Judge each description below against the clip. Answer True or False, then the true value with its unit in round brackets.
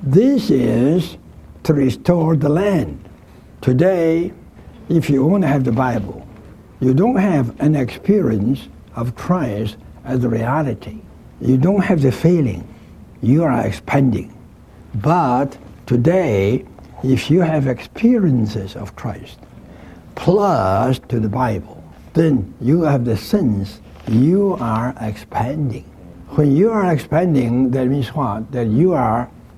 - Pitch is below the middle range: True (130 Hz)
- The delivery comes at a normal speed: False (125 wpm)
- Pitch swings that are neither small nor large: False (6.5 semitones)